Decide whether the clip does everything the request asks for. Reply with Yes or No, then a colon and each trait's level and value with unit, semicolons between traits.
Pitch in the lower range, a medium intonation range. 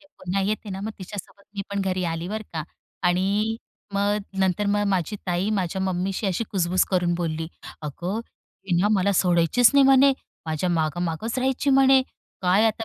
No: high, 190 Hz; average, 3.3 semitones